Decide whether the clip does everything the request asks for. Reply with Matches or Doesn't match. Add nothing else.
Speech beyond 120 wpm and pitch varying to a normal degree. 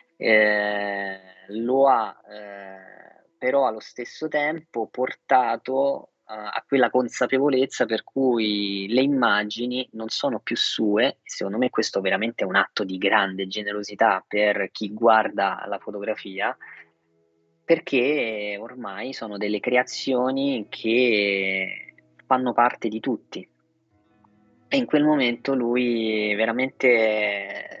Doesn't match